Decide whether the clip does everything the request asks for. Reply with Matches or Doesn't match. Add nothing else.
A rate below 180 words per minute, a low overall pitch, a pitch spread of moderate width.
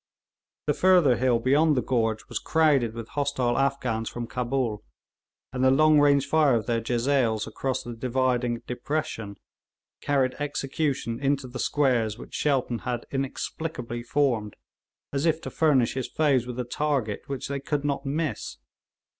Matches